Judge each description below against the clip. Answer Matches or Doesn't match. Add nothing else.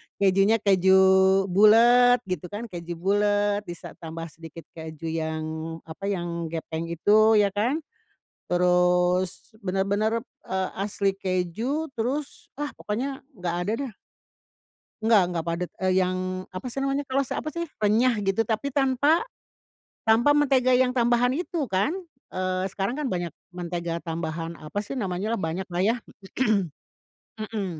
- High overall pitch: Matches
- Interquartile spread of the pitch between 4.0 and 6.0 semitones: Matches